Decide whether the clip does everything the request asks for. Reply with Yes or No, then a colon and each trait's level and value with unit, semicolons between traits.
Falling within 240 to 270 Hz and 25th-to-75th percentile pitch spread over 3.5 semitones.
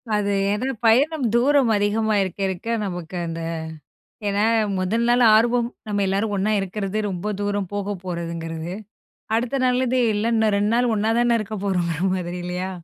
No: high, 205 Hz; average, 4.0 semitones